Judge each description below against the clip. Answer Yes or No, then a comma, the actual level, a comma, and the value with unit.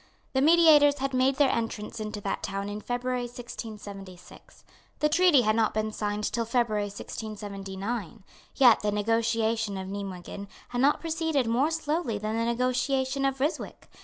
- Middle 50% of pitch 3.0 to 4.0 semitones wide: No, average, 4.4 semitones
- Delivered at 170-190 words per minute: No, average, 155 wpm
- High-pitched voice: Yes, high, 230 Hz